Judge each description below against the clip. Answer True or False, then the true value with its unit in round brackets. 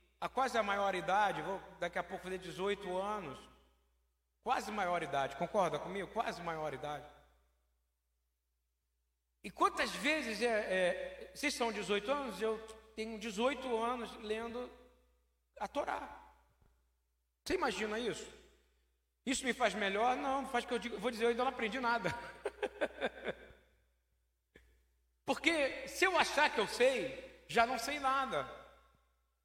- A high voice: True (195 Hz)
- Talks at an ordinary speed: True (130 wpm)